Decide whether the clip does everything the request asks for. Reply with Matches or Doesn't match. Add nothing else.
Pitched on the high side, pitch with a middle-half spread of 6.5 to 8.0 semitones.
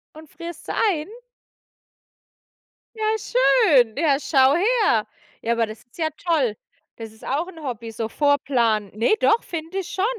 Matches